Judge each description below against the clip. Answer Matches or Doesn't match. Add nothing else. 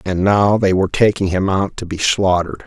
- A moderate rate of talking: Doesn't match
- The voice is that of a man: Matches